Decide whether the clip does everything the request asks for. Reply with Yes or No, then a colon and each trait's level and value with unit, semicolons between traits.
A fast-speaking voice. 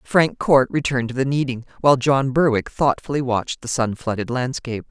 No: average, 185 wpm